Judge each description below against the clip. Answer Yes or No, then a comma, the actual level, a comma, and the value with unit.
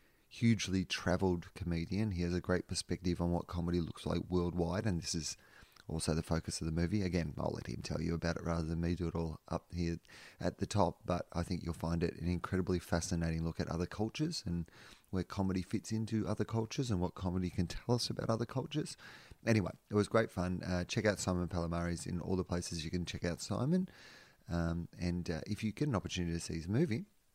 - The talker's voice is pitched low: Yes, very low, 90 Hz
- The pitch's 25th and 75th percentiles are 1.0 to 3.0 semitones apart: No, average, 3.6 semitones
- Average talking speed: No, fast, 225 wpm